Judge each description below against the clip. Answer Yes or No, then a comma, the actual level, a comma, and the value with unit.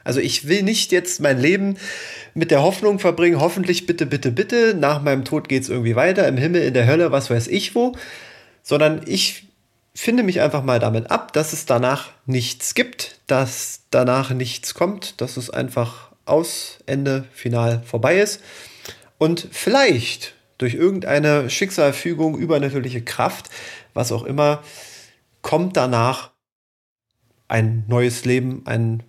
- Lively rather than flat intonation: Yes, wide, 5.9 semitones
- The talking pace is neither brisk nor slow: Yes, average, 150 wpm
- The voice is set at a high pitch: No, medium, 140 Hz